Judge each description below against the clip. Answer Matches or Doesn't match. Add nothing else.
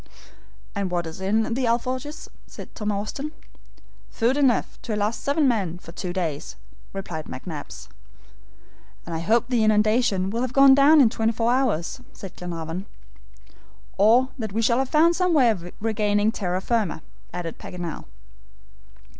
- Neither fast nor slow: Matches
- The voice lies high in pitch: Matches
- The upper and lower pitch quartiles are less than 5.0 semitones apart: Doesn't match